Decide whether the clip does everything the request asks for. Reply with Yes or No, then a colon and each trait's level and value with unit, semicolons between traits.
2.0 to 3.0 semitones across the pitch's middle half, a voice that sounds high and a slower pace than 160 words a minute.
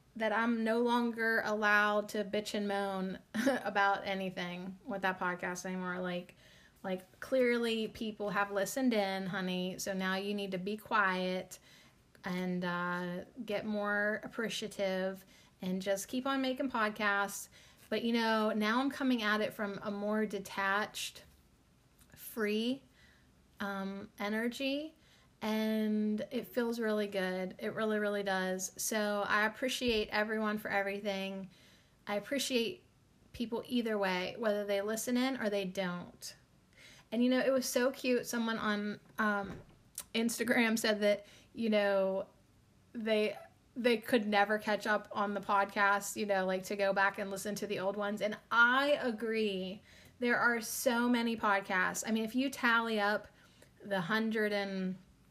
Yes: narrow, 2.6 semitones; high, 210 Hz; average, 150 wpm